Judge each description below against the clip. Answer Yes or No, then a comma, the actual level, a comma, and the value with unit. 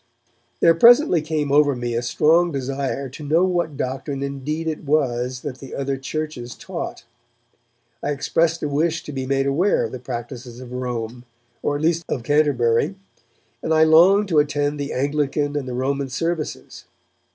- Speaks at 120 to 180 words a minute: Yes, average, 170 wpm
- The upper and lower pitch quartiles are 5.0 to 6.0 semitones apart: No, average, 3.4 semitones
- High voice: No, medium, 145 Hz